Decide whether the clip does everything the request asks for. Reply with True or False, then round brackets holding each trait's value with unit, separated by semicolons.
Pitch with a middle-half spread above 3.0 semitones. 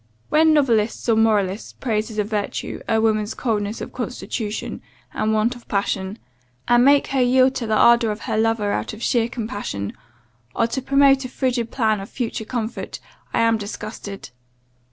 False (2.6 semitones)